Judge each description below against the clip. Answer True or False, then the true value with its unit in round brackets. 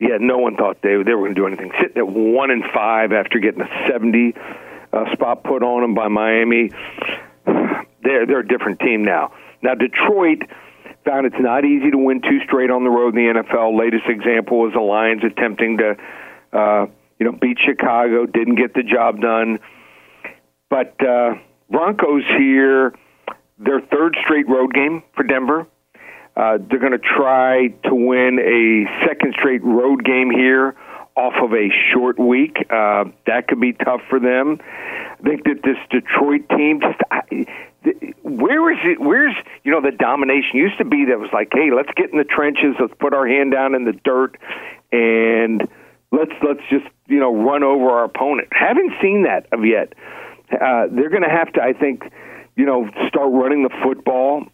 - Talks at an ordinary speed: True (180 wpm)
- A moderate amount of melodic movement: True (3.8 semitones)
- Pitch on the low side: True (130 Hz)